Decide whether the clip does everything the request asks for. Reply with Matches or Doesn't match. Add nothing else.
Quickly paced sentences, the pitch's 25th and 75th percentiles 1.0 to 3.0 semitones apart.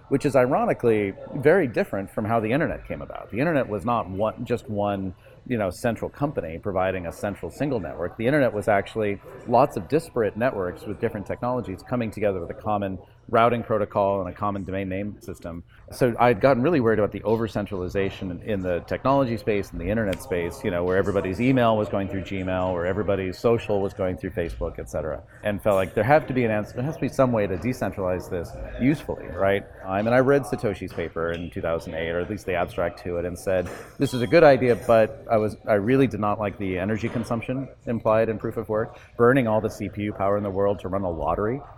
Doesn't match